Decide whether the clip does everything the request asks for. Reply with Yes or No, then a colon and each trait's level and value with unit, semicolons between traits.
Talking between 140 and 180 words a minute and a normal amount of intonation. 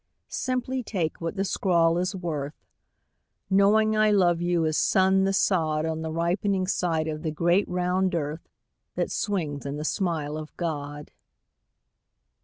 Yes: average, 150 wpm; average, 3.4 semitones